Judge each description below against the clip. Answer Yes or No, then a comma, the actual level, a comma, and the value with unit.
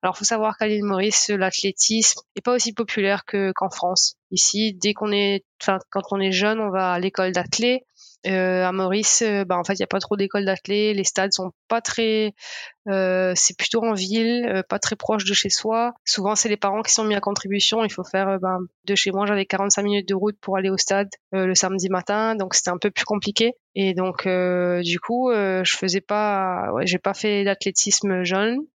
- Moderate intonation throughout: No, narrow, 2.2 semitones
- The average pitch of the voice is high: Yes, high, 200 Hz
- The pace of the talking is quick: Yes, fast, 225 wpm